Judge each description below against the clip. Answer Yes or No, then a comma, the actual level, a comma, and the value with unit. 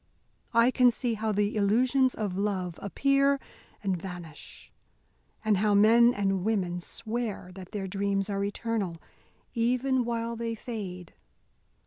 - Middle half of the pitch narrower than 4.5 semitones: Yes, average, 3.3 semitones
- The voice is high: Yes, high, 210 Hz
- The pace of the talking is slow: Yes, slow, 130 wpm